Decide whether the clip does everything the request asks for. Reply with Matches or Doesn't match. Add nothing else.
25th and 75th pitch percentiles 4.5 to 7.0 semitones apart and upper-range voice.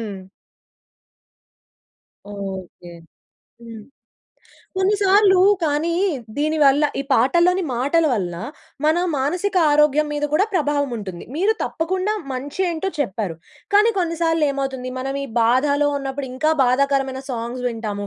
Matches